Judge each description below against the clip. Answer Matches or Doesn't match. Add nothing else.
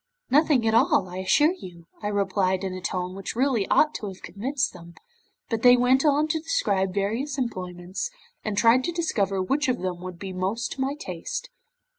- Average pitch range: Doesn't match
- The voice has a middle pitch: Doesn't match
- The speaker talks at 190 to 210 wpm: Matches